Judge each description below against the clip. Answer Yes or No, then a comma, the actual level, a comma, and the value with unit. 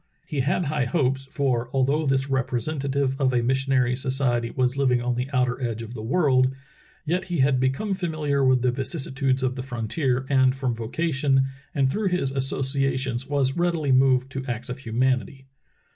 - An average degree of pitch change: No, narrow, 1.7 semitones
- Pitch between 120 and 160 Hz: Yes, low, 135 Hz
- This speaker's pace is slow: No, average, 175 wpm